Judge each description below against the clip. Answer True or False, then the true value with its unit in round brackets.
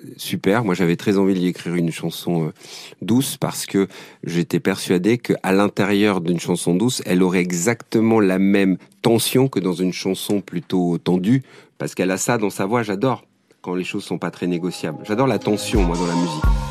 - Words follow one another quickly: False (190 wpm)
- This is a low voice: True (95 Hz)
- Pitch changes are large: False (3.2 semitones)